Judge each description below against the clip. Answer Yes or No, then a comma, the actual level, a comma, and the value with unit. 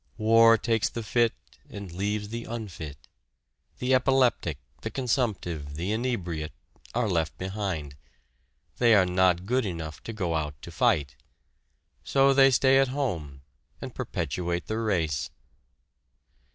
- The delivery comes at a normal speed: No, slow, 130 wpm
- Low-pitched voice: Yes, low, 100 Hz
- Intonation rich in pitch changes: Yes, wide, 6.1 semitones